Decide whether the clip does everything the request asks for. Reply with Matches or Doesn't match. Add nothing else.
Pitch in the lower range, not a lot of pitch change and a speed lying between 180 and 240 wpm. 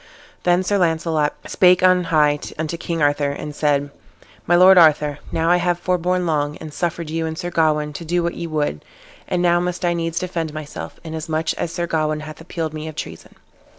Doesn't match